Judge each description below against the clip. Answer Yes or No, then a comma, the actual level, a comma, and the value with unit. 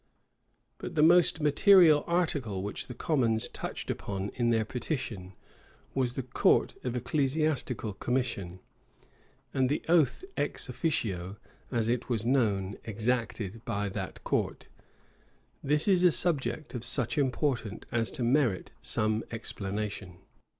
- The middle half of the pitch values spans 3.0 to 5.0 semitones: No, wide, 5.5 semitones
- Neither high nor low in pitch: No, low, 120 Hz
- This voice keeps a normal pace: No, slow, 130 wpm